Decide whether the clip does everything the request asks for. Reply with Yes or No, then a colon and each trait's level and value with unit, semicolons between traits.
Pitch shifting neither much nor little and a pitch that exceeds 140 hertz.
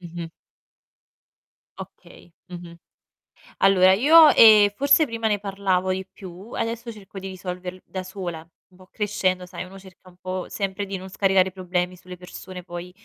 No: narrow, 1.8 semitones; medium, 185 Hz